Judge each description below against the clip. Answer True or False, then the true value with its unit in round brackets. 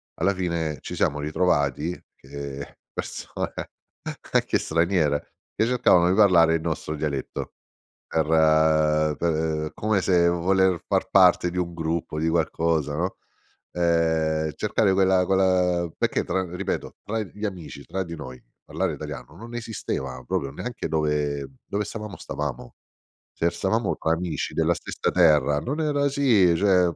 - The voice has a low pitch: True (85 Hz)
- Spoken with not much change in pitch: False (3.5 semitones)